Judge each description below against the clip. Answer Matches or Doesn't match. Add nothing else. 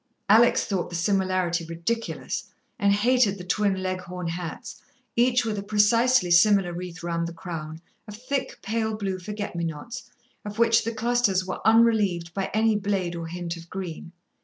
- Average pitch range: Matches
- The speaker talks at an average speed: Matches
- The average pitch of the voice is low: Doesn't match